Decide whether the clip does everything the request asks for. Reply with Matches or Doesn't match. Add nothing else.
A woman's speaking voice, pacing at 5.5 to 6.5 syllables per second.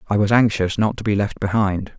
Doesn't match